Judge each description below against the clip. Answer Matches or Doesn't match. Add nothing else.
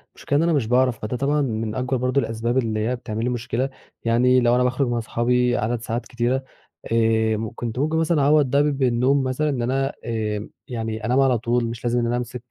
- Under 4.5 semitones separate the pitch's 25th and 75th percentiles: Matches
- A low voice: Matches